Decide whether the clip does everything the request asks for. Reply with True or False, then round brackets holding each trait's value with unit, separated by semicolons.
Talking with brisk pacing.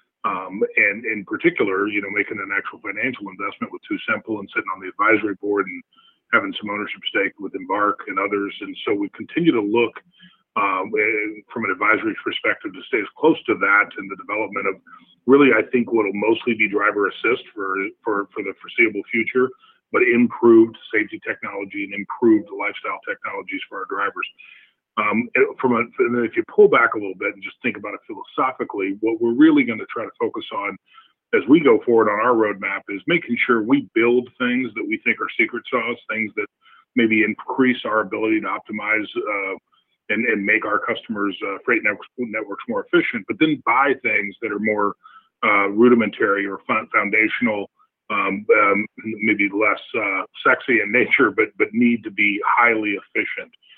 False (185 wpm)